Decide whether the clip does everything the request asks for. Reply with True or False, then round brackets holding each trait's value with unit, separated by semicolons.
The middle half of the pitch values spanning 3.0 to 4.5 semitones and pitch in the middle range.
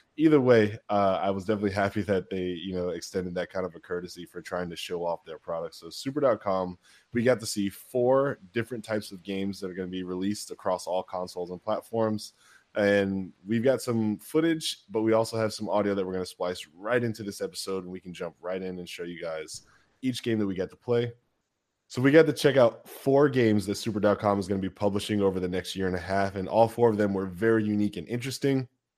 False (3.6 semitones; 100 Hz)